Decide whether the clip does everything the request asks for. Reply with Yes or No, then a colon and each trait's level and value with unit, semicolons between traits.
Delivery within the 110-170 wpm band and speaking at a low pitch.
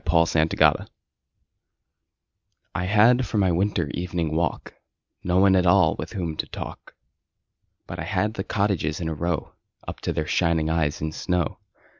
Yes: average, 160 wpm; very low, 85 Hz